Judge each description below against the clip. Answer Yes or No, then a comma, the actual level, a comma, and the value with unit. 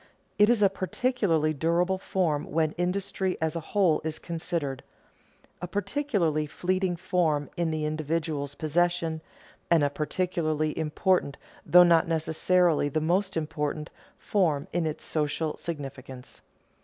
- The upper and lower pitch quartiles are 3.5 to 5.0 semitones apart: No, average, 2.9 semitones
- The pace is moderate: No, slow, 130 wpm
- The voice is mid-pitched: Yes, medium, 165 Hz